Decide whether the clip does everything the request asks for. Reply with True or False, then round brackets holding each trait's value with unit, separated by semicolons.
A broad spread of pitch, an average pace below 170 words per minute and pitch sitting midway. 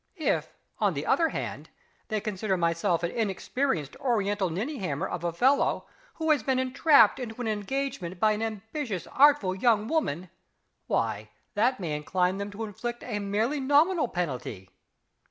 False (6.1 semitones; 155 wpm; 215 Hz)